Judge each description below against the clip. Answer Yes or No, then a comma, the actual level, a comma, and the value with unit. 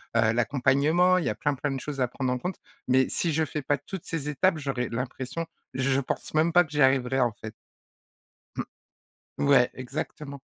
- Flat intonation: No, average, 3.2 semitones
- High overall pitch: No, low, 135 Hz